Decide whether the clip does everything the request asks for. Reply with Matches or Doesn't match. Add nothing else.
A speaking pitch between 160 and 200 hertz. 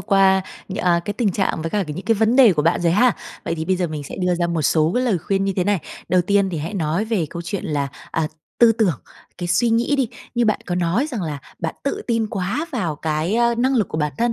Matches